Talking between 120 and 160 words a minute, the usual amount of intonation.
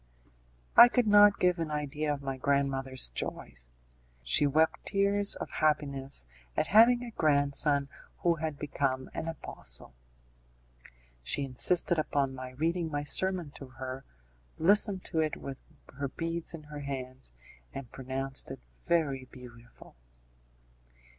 Yes: slow, 135 wpm; average, 3.9 semitones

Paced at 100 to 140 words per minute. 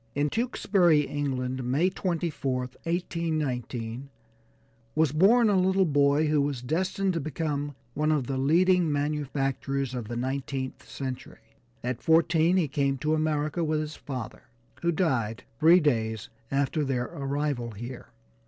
Yes: slow, 135 wpm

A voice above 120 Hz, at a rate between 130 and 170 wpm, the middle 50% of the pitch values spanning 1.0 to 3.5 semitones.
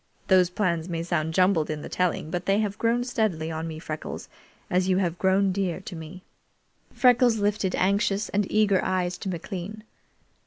No: medium, 185 Hz; average, 180 wpm; average, 3.0 semitones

